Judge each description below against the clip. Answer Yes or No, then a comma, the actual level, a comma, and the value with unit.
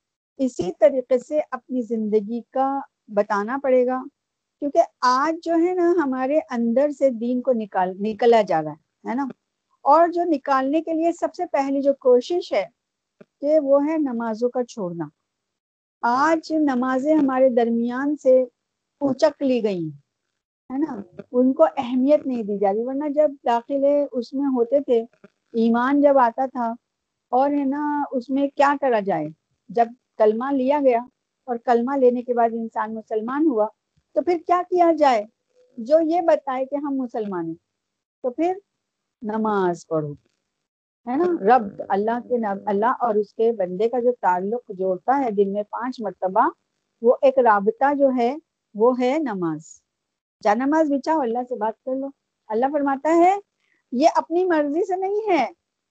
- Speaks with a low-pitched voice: No, very high, 260 Hz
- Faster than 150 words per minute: Yes, average, 160 wpm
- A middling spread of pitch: Yes, average, 4.4 semitones